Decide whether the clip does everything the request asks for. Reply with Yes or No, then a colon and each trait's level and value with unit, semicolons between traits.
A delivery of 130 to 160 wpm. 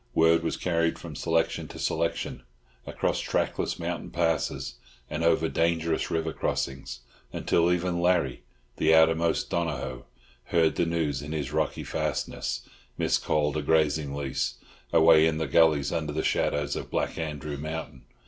Yes: average, 145 wpm